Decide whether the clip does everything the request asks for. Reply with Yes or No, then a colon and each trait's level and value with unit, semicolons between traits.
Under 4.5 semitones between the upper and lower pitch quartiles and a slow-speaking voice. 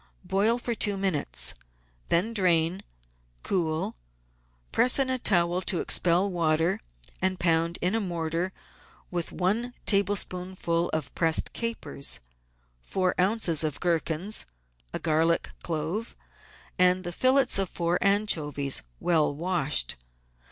Yes: average, 3.4 semitones; slow, 115 wpm